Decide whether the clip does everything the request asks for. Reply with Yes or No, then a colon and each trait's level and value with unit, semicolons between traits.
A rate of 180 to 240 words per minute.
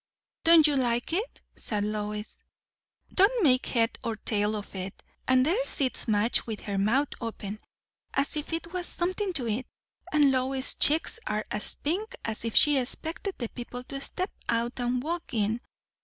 No: average, 170 wpm